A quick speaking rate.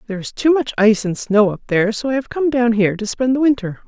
Yes: fast, 295 wpm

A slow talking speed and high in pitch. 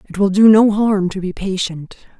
No: fast, 220 wpm; high, 195 Hz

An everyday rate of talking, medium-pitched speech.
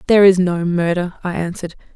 Yes: average, 185 wpm; medium, 180 Hz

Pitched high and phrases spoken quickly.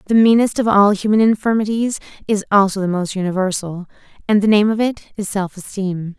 No: high, 200 Hz; average, 185 wpm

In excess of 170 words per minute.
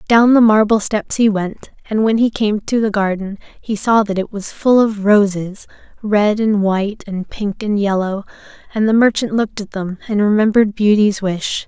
Yes: average, 195 wpm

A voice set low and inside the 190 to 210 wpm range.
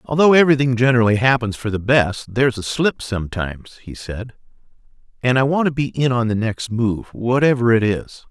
Yes: low, 120 Hz; average, 195 wpm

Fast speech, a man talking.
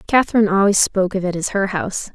No: fast, 225 wpm; female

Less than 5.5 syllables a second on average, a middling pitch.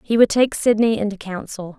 No: 5.3 syllables/s; high, 210 Hz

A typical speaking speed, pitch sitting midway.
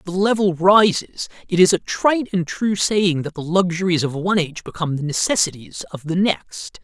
Yes: average, 195 wpm; medium, 180 Hz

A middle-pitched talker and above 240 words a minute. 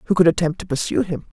Yes: medium, 165 Hz; fast, 255 wpm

